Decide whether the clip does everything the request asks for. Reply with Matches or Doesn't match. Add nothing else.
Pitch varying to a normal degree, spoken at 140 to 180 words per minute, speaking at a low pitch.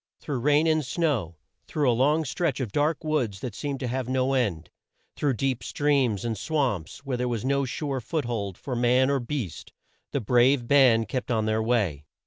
Doesn't match